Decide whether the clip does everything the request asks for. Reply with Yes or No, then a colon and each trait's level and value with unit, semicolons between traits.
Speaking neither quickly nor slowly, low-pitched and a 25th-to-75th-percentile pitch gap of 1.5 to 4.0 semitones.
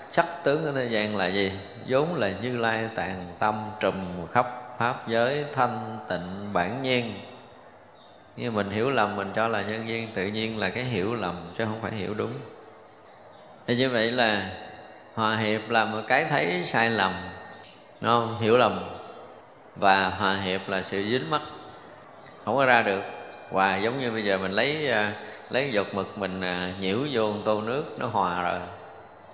Yes: average, 175 wpm; low, 110 Hz; average, 3.7 semitones